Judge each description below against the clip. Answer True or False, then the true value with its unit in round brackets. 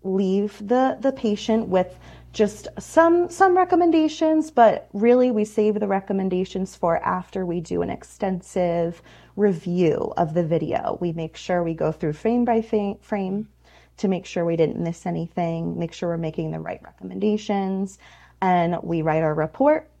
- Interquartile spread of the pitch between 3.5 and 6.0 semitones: True (4.5 semitones)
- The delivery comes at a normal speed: True (160 wpm)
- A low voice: False (190 Hz)